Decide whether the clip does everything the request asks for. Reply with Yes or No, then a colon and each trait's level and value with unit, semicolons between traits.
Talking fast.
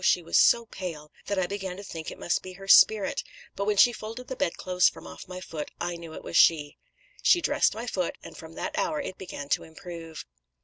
Yes: fast, 230 wpm